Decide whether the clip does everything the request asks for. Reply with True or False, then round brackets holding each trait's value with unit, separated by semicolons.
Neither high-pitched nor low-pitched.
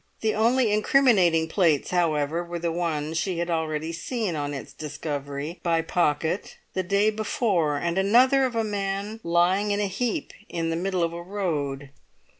True (175 Hz)